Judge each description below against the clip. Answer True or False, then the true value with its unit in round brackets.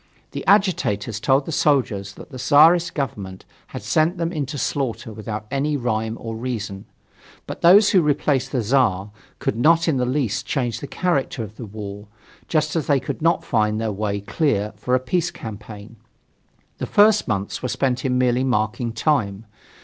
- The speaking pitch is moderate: False (125 Hz)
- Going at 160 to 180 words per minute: True (175 wpm)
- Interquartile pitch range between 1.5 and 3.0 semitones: False (5.6 semitones)